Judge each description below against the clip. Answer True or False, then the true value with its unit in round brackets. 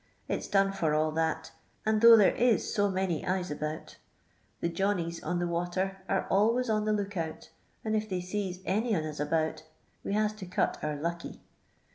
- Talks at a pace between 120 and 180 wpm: False (195 wpm)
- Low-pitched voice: False (185 Hz)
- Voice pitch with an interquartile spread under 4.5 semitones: True (3.9 semitones)